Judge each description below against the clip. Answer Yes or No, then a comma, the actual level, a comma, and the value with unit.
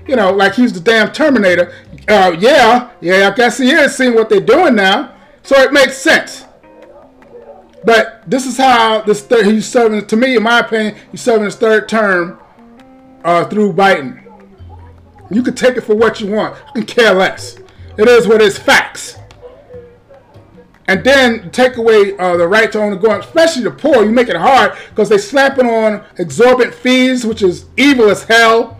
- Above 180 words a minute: Yes, average, 190 wpm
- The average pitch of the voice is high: Yes, high, 225 Hz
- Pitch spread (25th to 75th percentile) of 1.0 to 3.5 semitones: No, average, 4.1 semitones